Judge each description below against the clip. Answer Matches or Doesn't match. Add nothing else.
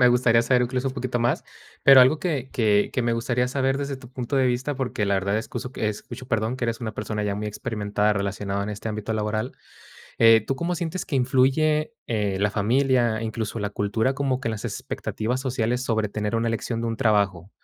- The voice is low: Matches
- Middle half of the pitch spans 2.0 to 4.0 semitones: Matches